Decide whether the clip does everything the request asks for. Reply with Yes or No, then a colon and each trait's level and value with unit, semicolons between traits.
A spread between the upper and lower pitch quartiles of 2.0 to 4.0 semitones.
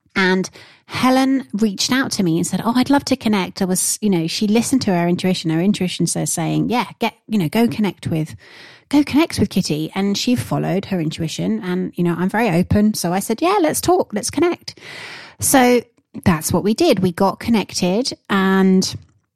No: wide, 5.4 semitones